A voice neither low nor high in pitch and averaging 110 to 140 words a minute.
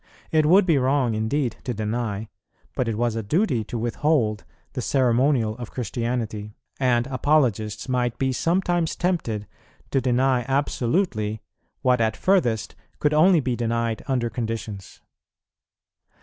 No: low, 120 Hz; slow, 135 wpm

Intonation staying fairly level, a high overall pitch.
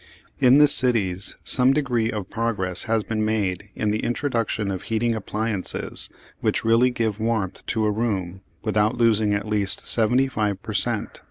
No: narrow, 2.2 semitones; low, 110 Hz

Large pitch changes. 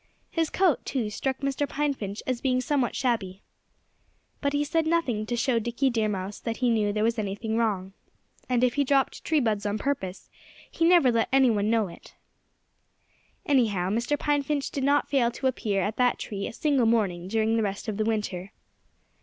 No: average, 4.6 semitones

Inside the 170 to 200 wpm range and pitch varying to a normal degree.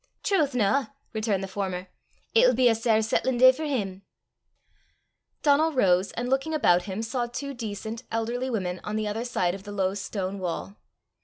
Yes: average, 175 wpm; average, 4.8 semitones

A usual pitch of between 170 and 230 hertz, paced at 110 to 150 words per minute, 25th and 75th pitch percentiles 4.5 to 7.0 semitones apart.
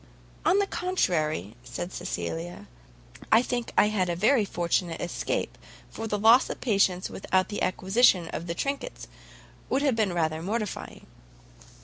Yes: high, 190 Hz; average, 145 wpm; average, 5.3 semitones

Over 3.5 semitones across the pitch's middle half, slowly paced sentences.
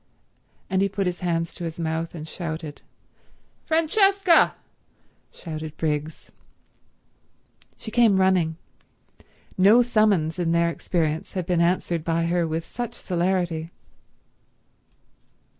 No: average, 3.2 semitones; slow, 110 wpm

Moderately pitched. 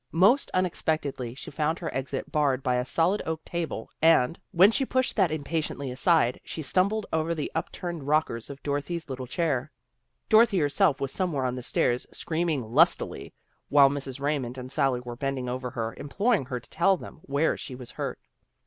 Yes: medium, 145 Hz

